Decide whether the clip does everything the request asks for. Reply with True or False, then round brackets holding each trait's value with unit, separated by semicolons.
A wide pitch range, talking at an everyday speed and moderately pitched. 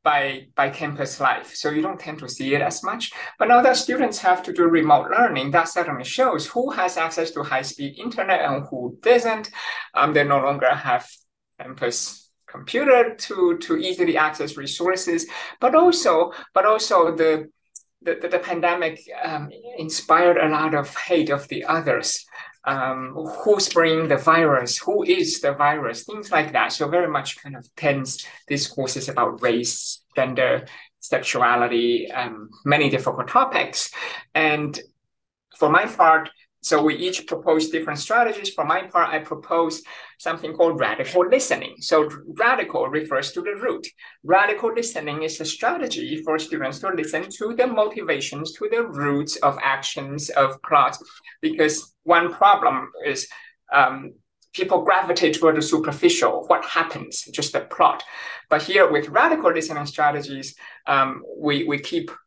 True (7.4 semitones; 155 wpm; 160 Hz)